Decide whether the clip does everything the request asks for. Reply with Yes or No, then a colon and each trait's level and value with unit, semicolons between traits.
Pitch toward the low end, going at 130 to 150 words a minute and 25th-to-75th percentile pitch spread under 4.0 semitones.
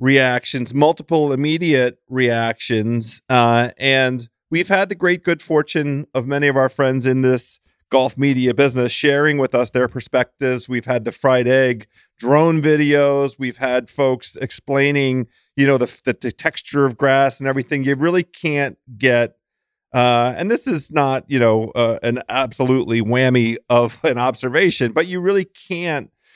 No: low, 130 Hz; average, 160 wpm; average, 2.7 semitones